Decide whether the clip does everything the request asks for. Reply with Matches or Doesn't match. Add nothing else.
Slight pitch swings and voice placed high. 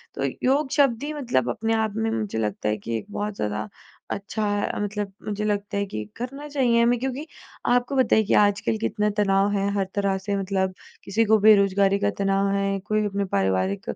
Matches